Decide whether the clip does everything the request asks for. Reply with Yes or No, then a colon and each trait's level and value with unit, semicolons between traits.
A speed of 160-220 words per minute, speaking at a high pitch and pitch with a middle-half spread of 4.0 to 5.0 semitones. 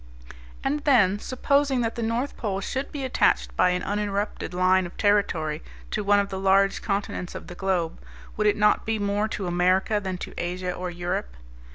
No: average, 190 wpm; high, 200 Hz; average, 3.0 semitones